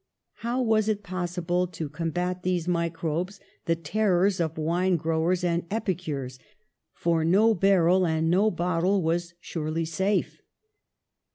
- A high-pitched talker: No, medium, 175 Hz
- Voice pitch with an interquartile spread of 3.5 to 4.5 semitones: No, narrow, 2.4 semitones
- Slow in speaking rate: No, average, 145 wpm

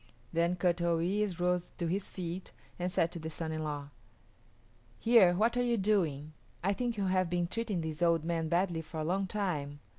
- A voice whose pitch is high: No, medium, 175 Hz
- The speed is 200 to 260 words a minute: Yes, fast, 205 wpm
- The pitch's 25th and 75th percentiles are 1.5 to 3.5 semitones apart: Yes, average, 3.0 semitones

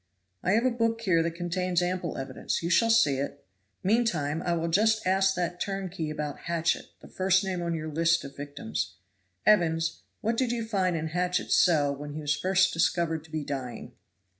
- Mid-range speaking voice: Yes, medium, 170 Hz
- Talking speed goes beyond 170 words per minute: Yes, average, 190 wpm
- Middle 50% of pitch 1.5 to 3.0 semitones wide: No, average, 3.6 semitones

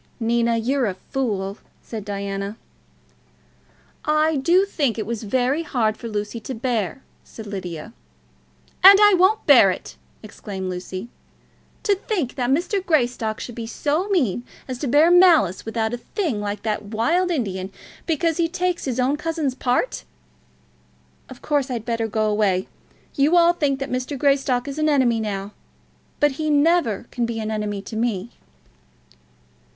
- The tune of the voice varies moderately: No, wide, 6.0 semitones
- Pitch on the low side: No, high, 245 Hz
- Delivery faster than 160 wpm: No, average, 155 wpm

